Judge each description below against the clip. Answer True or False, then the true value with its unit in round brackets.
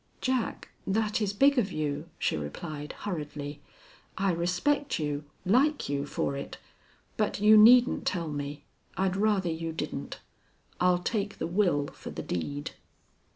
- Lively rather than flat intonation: True (6.3 semitones)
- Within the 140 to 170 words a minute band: True (145 wpm)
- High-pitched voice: False (180 Hz)